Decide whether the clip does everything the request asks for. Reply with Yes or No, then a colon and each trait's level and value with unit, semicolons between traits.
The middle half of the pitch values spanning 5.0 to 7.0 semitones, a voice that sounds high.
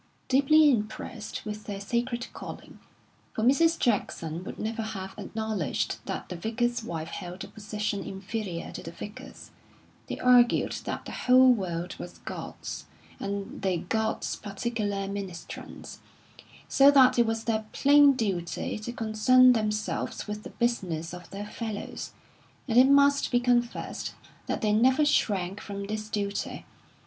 No: average, 3.5 semitones; high, 215 Hz